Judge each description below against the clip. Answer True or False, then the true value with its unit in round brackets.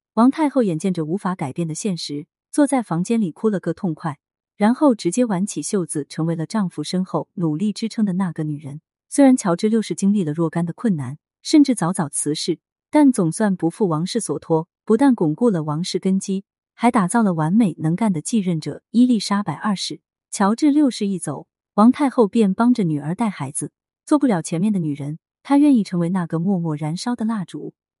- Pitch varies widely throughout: True (5.7 semitones)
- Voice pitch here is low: False (190 Hz)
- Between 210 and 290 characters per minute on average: False (305 characters per minute)